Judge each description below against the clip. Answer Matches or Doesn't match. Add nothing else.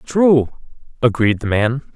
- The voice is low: Matches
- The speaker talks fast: Doesn't match